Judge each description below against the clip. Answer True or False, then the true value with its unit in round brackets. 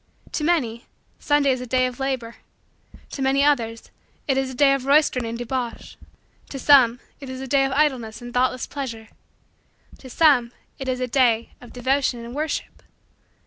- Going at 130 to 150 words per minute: False (180 wpm)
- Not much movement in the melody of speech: True (2.3 semitones)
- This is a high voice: True (260 Hz)